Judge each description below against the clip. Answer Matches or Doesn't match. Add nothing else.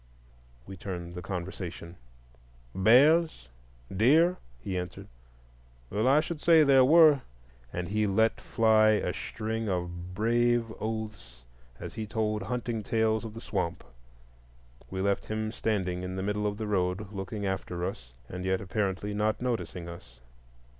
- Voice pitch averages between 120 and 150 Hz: Doesn't match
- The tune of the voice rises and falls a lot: Doesn't match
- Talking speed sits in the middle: Matches